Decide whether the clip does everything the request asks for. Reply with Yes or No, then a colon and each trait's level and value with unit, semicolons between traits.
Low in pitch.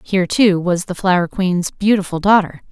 No: medium, 185 Hz